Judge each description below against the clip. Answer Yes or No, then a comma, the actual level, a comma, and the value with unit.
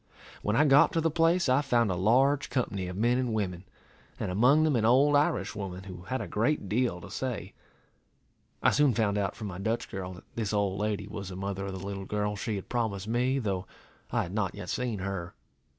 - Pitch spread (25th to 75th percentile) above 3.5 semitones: Yes, average, 4.5 semitones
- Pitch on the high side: No, low, 105 Hz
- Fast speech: Yes, fast, 225 wpm